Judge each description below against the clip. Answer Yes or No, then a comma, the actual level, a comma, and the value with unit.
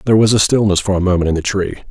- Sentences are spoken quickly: Yes, fast, 285 wpm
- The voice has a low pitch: Yes, low, 100 Hz